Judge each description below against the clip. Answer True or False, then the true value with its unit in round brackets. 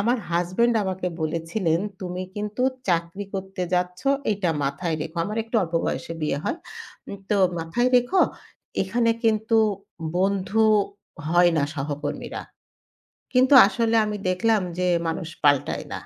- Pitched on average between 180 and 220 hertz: True (185 Hz)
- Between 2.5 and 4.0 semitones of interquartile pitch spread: False (4.7 semitones)